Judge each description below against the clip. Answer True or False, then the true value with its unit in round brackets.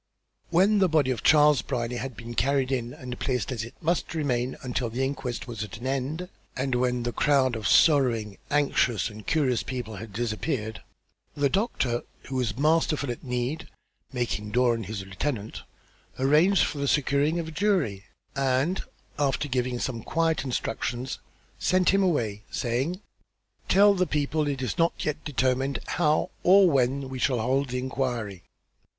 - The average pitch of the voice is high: False (130 Hz)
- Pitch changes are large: False (3.7 semitones)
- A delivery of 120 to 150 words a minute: False (165 wpm)